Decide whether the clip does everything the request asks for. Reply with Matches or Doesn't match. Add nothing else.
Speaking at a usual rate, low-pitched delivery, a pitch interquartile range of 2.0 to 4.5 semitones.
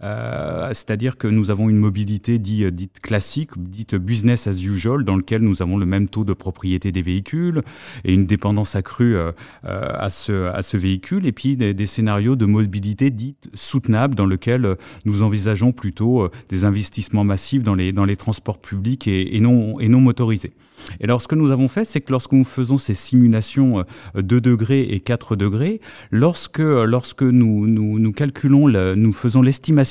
Matches